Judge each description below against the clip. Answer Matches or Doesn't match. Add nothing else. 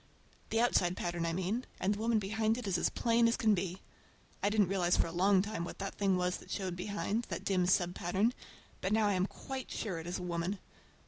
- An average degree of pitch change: Matches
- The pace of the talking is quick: Matches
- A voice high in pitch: Matches